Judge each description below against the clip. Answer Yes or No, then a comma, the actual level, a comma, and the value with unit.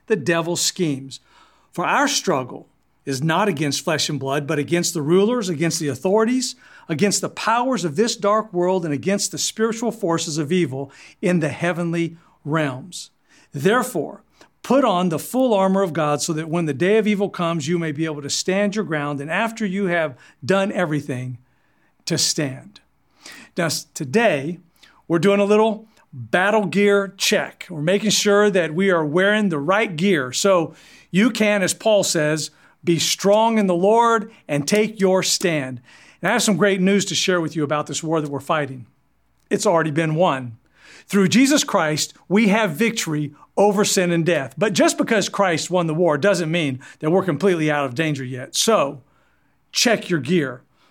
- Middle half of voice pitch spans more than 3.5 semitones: Yes, average, 4.7 semitones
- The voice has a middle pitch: Yes, medium, 180 Hz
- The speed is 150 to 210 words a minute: Yes, average, 180 wpm